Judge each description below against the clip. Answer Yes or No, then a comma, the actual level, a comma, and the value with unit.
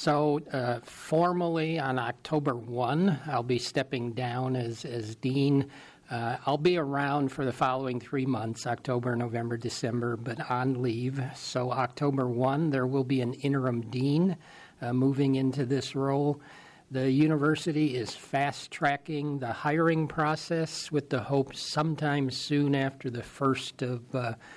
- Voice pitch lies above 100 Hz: Yes, low, 135 Hz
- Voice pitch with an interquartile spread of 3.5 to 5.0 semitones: No, average, 3.0 semitones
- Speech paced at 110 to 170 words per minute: Yes, average, 145 wpm